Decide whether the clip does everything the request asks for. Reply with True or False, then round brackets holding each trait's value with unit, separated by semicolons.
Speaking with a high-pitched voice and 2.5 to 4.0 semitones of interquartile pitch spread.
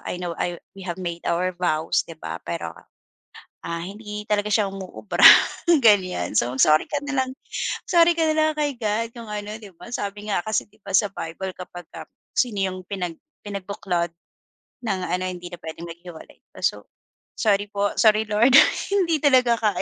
True (200 Hz; 3.7 semitones)